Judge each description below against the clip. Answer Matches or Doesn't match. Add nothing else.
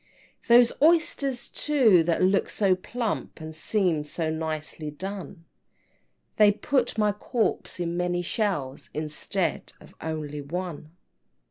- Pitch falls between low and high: Matches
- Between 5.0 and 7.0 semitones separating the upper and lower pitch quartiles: Matches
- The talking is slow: Matches